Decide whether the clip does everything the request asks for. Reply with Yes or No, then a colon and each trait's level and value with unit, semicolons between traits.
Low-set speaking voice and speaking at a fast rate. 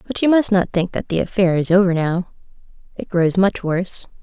No: medium, 185 Hz; fast, 215 wpm